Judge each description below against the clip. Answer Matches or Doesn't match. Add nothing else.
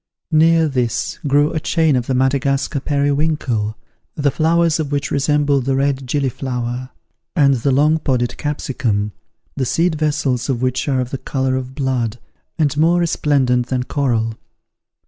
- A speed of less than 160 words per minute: Matches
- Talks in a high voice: Doesn't match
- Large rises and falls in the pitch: Doesn't match